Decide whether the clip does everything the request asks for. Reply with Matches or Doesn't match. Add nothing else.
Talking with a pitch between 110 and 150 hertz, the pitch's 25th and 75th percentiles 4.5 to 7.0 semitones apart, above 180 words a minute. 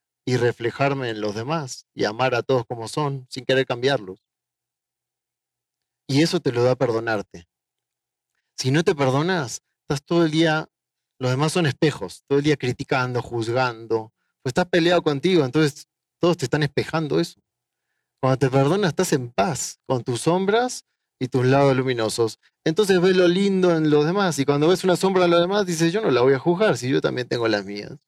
Matches